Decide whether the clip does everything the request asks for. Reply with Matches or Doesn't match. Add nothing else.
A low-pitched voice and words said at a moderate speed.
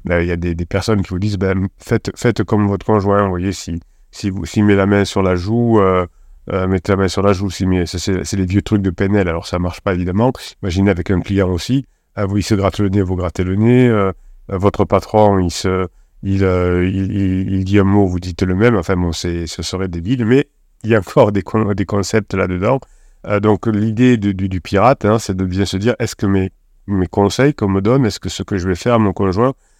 Doesn't match